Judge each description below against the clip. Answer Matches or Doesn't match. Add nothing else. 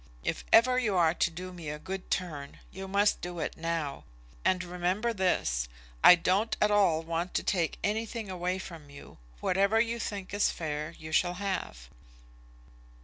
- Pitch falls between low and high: Matches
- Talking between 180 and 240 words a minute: Doesn't match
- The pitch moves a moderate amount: Matches